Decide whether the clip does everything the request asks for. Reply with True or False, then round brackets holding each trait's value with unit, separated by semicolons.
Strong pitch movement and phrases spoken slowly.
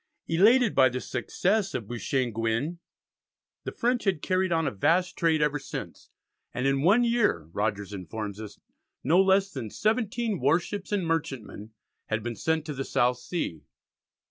False (8.6 semitones; 160 wpm)